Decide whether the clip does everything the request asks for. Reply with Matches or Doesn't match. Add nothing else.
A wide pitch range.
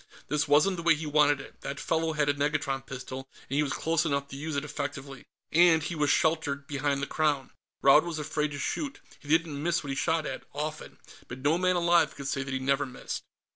Doesn't match